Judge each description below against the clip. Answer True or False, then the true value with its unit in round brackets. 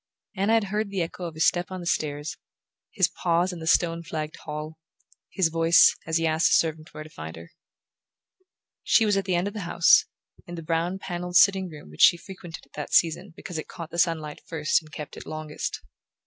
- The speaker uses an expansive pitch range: False (2.4 semitones)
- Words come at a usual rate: False (220 wpm)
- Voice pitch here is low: False (165 Hz)